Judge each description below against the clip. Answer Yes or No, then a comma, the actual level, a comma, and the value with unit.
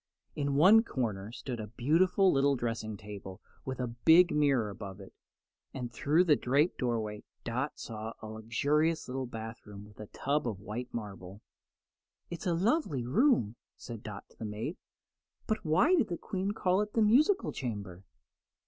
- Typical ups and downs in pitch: No, wide, 7.4 semitones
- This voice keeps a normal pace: Yes, average, 165 wpm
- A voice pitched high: No, low, 125 Hz